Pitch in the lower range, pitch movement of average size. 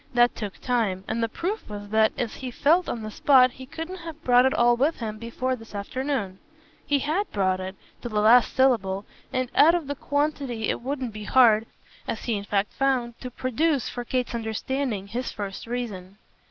No: high, 240 Hz; average, 3.9 semitones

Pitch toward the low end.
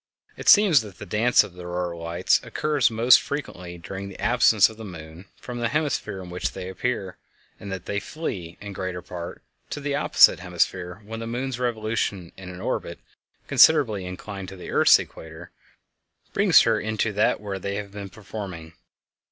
Yes: low, 100 Hz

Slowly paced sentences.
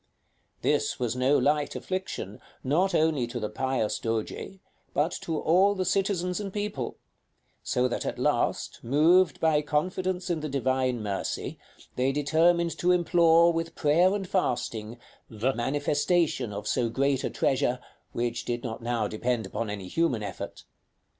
No: average, 150 wpm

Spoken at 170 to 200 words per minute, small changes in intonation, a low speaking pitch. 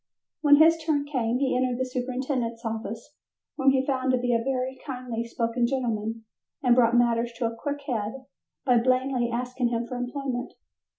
No: average, 175 wpm; narrow, 2.1 semitones; very high, 250 Hz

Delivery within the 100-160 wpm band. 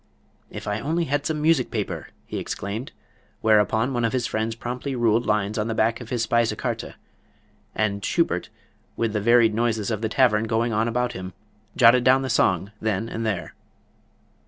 No: average, 180 wpm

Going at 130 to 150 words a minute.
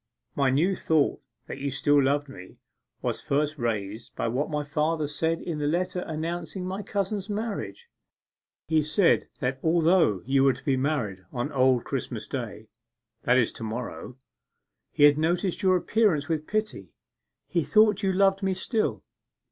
No: average, 165 wpm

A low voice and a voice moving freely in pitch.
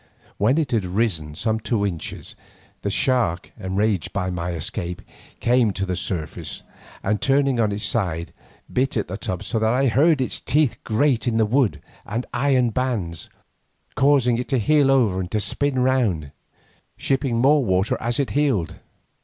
Yes: low, 115 Hz; wide, 5.7 semitones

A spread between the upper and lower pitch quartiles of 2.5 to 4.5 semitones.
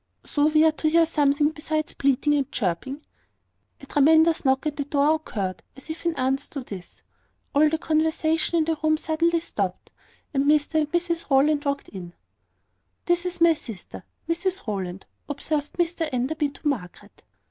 Yes: average, 2.8 semitones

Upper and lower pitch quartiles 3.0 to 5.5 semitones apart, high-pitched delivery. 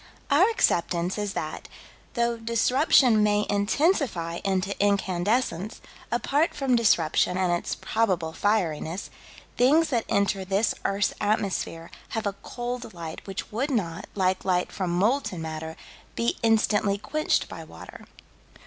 Yes: average, 4.6 semitones; high, 205 Hz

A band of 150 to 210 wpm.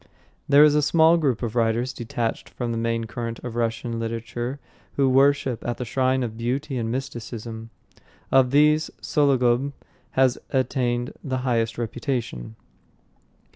No: average, 140 wpm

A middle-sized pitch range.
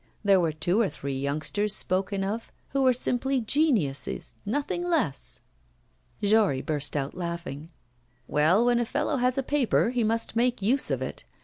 No: wide, 7.5 semitones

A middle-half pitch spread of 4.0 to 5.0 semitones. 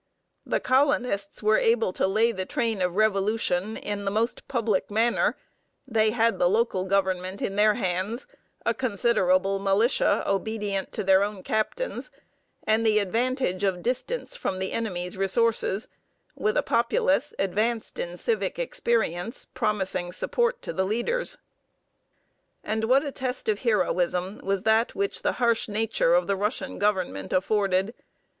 No: average, 3.5 semitones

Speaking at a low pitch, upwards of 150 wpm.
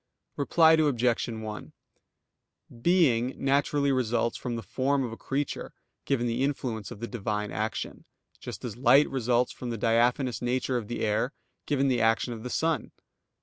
Yes: low, 125 Hz; average, 160 wpm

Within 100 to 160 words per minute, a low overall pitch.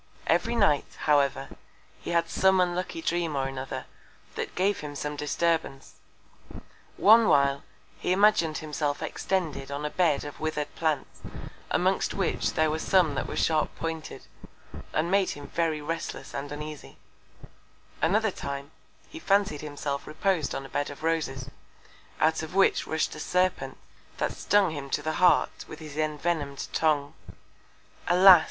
No: average, 150 wpm; medium, 155 Hz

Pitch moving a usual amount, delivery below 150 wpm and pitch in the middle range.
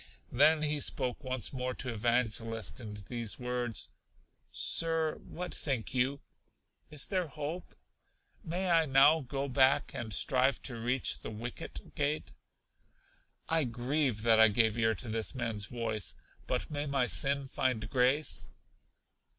No: average, 3.9 semitones; average, 140 wpm; low, 130 Hz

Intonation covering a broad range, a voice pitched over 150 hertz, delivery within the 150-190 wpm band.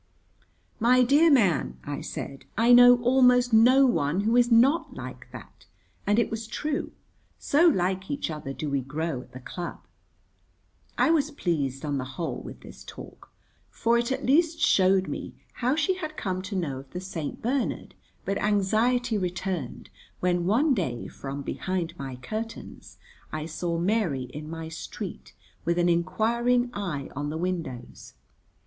Yes: wide, 7.8 semitones; high, 190 Hz; average, 160 wpm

